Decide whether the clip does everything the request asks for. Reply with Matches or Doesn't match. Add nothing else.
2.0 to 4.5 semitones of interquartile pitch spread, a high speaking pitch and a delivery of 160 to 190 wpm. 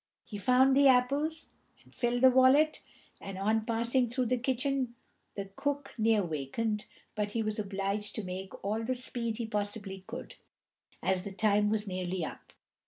Matches